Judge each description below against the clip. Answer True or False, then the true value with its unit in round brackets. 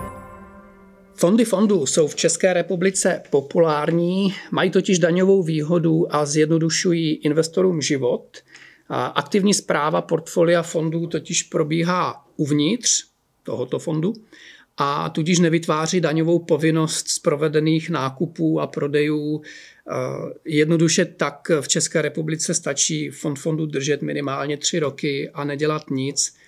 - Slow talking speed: True (110 wpm)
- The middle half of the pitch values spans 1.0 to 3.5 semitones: True (2.6 semitones)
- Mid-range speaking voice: True (160 Hz)